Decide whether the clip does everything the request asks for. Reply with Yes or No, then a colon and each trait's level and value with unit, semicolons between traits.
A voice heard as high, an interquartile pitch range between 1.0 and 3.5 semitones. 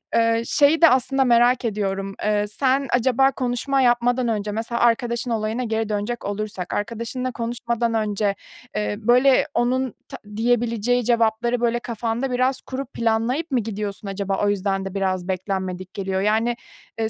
Yes: high, 230 Hz; average, 3.0 semitones